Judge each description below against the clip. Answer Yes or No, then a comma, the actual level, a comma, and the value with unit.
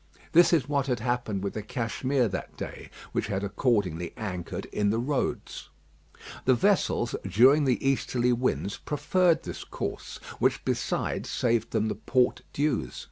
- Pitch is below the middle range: Yes, low, 120 Hz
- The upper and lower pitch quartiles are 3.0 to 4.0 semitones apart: No, average, 4.7 semitones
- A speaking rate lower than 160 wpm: Yes, average, 150 wpm